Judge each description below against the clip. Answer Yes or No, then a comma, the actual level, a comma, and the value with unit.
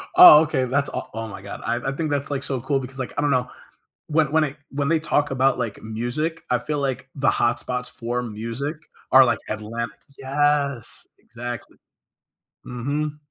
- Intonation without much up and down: No, average, 3.3 semitones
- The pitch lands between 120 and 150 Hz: Yes, low, 135 Hz